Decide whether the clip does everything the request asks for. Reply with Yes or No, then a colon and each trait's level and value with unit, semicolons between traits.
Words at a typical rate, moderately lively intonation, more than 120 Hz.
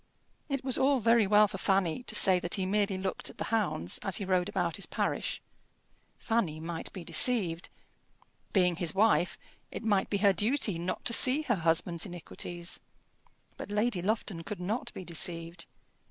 Yes: average, 175 wpm; average, 3.8 semitones; high, 190 Hz